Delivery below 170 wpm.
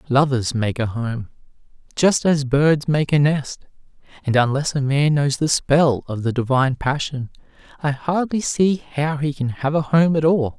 No: average, 180 wpm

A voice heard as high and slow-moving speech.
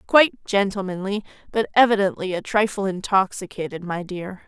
Yes: high, 195 Hz; slow, 120 wpm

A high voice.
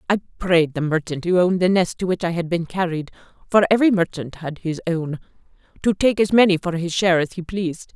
No: medium, 175 Hz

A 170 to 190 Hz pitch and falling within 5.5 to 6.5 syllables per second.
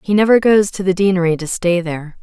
Yes: medium, 185 Hz; 6.2 syllables/s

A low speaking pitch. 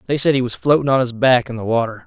Yes: low, 125 Hz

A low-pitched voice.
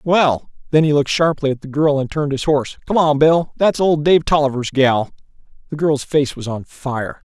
No: medium, 145 Hz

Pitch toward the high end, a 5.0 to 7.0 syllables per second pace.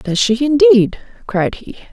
No: high, 240 Hz; 4.1 syllables/s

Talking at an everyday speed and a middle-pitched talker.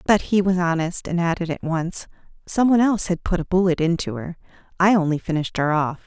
No: fast, 220 wpm; medium, 175 Hz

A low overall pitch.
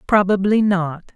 No: high, 190 Hz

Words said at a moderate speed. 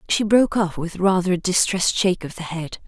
No: fast, 230 wpm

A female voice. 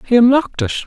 No: male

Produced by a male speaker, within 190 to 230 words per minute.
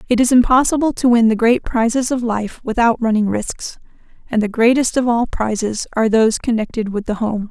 No: female; average, 200 wpm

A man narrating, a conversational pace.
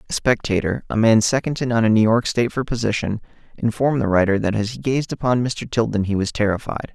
No: male; fast, 225 wpm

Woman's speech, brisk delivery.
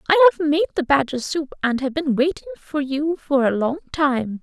Yes: female; fast, 215 wpm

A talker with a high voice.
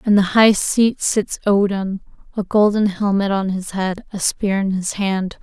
Yes: high, 200 Hz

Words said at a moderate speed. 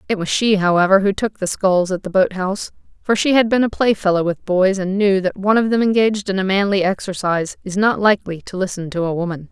No: fast, 245 wpm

